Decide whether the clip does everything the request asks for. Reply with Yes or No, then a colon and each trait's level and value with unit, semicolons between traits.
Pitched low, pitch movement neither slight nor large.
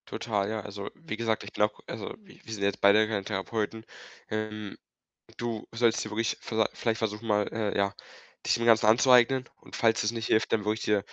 No: low, 110 Hz; narrow, 1.5 semitones